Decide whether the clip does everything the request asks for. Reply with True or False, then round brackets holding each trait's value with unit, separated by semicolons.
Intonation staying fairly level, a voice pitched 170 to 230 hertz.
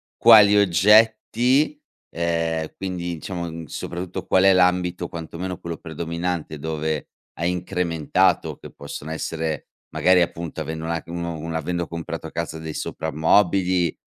False (2.2 semitones; 85 Hz)